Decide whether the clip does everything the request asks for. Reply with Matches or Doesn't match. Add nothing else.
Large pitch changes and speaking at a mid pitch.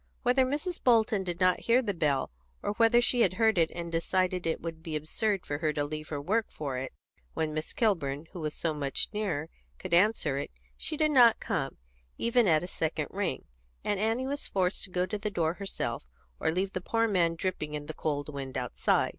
Matches